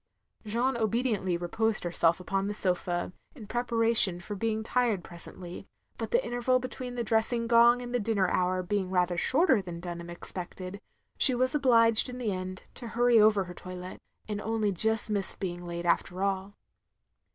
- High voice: Yes, high, 210 Hz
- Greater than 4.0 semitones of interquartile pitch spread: Yes, average, 4.4 semitones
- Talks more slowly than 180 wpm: Yes, average, 165 wpm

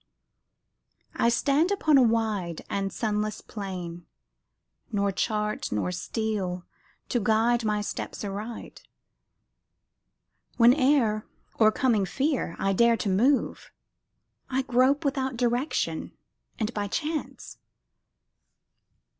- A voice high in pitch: Yes, high, 220 Hz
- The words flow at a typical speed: No, slow, 95 wpm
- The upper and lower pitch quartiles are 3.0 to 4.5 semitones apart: Yes, average, 4.2 semitones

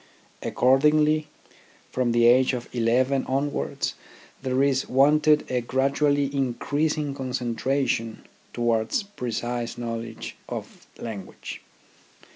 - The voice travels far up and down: No, average, 3.0 semitones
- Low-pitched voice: Yes, low, 130 Hz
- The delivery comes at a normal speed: No, slow, 100 wpm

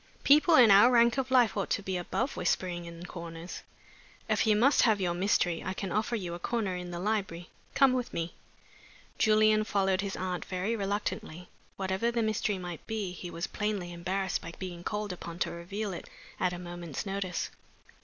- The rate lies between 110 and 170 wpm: No, average, 190 wpm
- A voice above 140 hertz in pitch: Yes, high, 190 Hz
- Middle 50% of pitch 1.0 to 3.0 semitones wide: No, average, 3.5 semitones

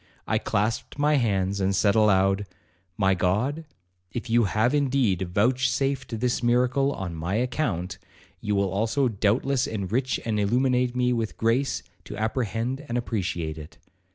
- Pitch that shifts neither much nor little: Yes, average, 4.4 semitones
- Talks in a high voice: No, low, 115 Hz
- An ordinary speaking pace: Yes, average, 145 wpm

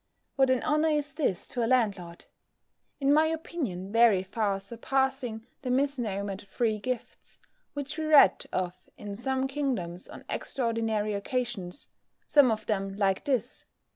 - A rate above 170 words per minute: No, average, 145 wpm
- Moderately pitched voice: No, high, 235 Hz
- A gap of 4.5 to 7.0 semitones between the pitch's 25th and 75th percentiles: Yes, average, 5.2 semitones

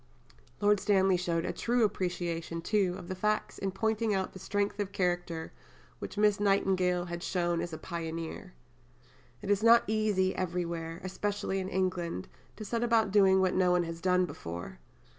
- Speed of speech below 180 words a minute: Yes, average, 170 wpm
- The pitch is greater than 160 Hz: Yes, medium, 185 Hz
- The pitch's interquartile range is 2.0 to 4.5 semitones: Yes, average, 2.9 semitones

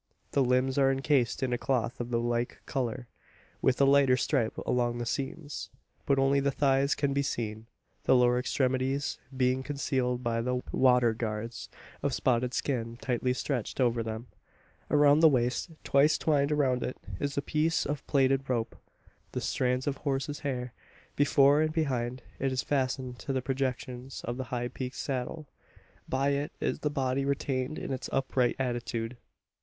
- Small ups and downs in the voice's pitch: Yes, narrow, 2.1 semitones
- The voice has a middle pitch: No, low, 130 Hz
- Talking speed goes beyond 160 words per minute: Yes, average, 170 wpm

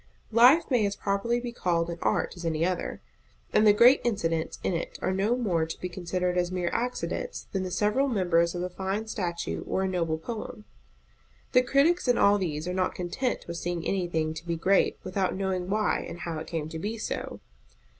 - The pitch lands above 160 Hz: Yes, medium, 185 Hz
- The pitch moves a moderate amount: Yes, average, 4.1 semitones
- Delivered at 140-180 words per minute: No, fast, 205 wpm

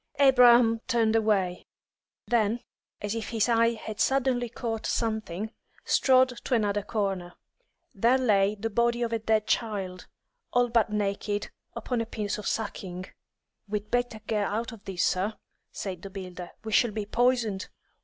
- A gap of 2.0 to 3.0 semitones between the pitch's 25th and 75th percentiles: Yes, average, 2.7 semitones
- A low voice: No, high, 220 Hz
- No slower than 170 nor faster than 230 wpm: No, average, 155 wpm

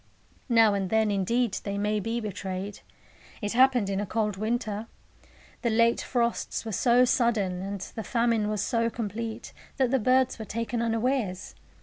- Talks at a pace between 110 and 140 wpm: No, average, 160 wpm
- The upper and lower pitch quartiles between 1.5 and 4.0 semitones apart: Yes, narrow, 2.6 semitones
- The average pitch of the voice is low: No, high, 225 Hz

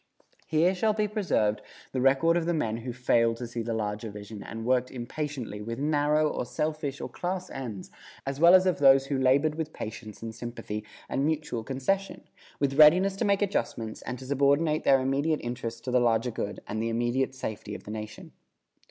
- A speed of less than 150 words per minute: No, average, 195 wpm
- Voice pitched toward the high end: No, low, 135 Hz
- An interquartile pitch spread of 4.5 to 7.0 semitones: Yes, average, 5.1 semitones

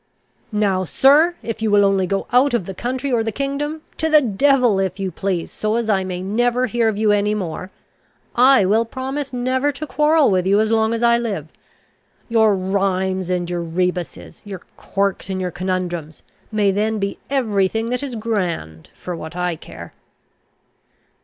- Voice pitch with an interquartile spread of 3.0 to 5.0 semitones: Yes, average, 4.7 semitones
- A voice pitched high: Yes, high, 205 Hz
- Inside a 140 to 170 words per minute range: No, average, 185 wpm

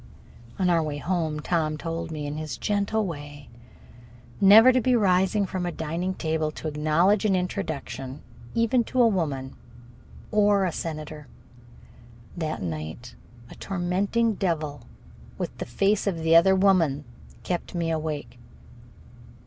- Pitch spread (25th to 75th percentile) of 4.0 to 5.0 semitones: Yes, average, 4.3 semitones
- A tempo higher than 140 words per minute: No, slow, 135 wpm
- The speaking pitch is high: No, medium, 170 Hz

